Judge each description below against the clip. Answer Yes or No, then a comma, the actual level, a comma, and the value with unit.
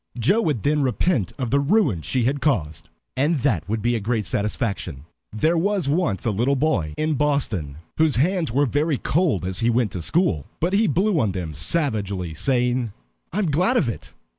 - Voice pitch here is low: Yes, low, 130 Hz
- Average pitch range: No, wide, 7.3 semitones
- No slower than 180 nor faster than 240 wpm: Yes, average, 195 wpm